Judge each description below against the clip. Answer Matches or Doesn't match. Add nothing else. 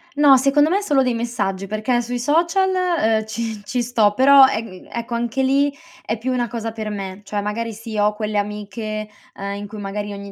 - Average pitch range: Matches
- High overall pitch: Matches